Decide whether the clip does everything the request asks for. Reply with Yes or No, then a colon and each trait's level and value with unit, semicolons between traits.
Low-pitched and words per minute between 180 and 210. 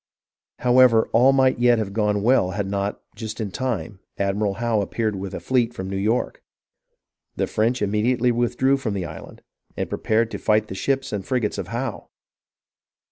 Yes: low, 110 Hz; average, 190 wpm